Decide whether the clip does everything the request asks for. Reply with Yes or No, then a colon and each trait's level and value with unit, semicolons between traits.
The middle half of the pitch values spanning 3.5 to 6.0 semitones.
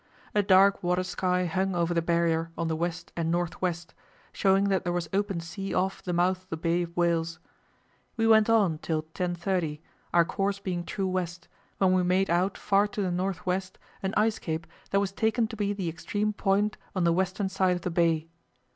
No: narrow, 2.4 semitones